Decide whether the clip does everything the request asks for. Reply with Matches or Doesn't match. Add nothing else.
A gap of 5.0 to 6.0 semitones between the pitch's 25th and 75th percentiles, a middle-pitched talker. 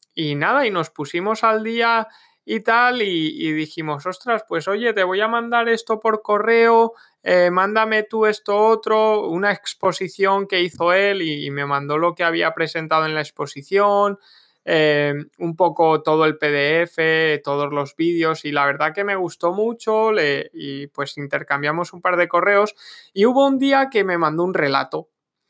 Matches